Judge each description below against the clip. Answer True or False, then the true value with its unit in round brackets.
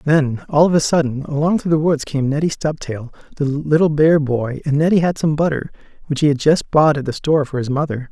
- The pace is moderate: False (235 wpm)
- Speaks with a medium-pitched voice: True (150 Hz)